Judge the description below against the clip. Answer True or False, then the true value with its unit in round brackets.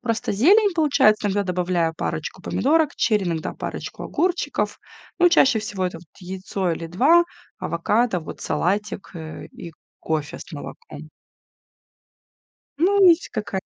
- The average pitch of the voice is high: True (210 Hz)